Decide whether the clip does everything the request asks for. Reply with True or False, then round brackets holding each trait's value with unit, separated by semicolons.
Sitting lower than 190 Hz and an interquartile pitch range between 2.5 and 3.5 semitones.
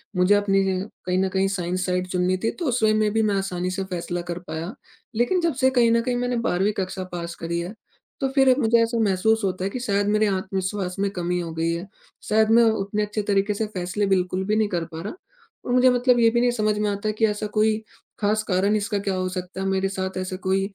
False (195 Hz; 3.0 semitones)